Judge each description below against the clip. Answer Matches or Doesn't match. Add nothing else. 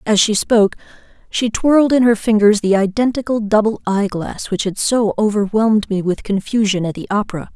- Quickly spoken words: Doesn't match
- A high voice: Matches